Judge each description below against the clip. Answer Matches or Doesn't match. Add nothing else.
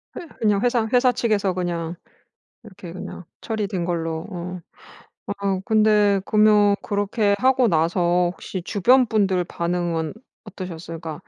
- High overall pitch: Matches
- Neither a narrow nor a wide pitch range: Matches